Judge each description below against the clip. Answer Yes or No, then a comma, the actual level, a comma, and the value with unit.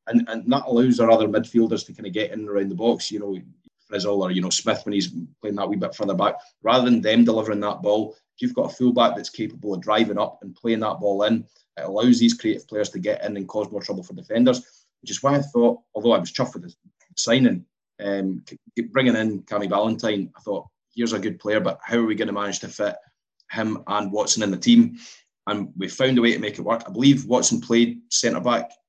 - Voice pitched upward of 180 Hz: No, low, 115 Hz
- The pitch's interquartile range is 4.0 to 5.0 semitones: Yes, average, 4.6 semitones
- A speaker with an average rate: No, fast, 245 wpm